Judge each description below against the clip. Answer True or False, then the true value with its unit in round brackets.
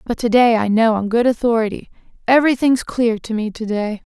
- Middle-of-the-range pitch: False (230 Hz)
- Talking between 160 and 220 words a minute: True (205 wpm)